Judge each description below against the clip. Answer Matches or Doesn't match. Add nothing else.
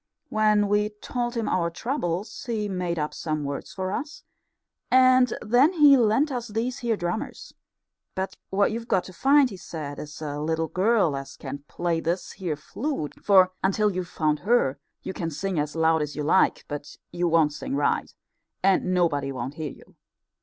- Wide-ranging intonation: Matches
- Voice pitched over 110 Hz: Matches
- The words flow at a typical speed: Matches